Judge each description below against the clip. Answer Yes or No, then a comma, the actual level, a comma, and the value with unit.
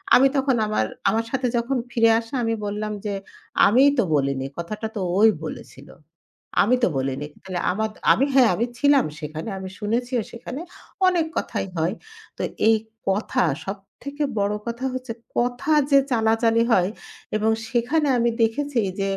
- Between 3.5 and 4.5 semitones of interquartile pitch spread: Yes, average, 3.9 semitones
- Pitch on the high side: Yes, high, 225 Hz